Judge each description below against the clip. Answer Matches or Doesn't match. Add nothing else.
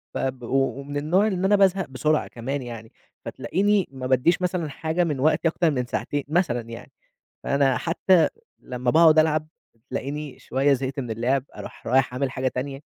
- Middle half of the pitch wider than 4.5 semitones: Doesn't match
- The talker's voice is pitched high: Doesn't match